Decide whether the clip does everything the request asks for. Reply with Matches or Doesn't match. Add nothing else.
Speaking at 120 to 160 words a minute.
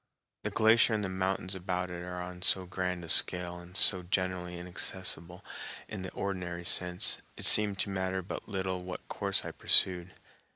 Doesn't match